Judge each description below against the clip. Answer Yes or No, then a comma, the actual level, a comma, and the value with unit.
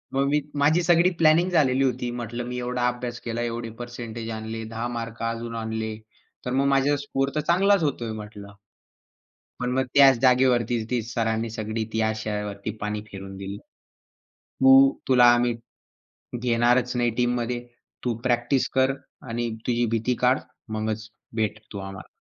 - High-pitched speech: No, low, 120 Hz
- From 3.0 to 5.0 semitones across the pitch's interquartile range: No, narrow, 2.4 semitones